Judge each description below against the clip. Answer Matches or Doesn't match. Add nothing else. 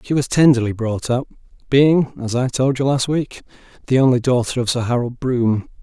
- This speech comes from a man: Matches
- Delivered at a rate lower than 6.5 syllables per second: Matches